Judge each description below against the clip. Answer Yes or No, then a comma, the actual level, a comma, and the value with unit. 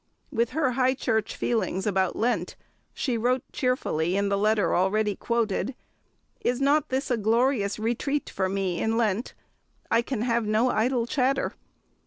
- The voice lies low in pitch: No, high, 230 Hz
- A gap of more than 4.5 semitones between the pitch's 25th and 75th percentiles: No, average, 3.6 semitones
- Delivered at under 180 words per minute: Yes, average, 155 wpm